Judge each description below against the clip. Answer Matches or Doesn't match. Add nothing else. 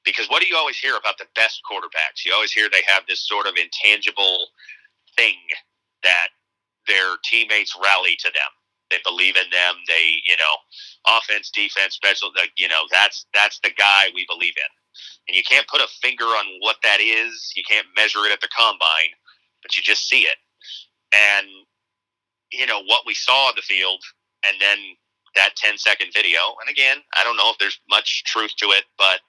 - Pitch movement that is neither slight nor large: Doesn't match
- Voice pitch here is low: Matches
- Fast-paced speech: Doesn't match